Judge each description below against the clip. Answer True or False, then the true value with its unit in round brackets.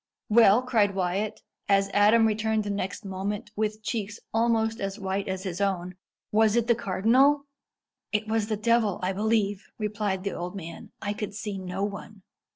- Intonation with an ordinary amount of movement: False (2.2 semitones)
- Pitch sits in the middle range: False (210 Hz)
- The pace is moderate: True (170 wpm)